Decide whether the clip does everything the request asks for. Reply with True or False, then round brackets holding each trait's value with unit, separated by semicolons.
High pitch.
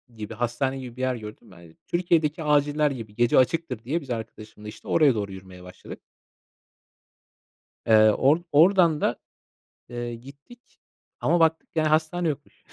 False (130 Hz)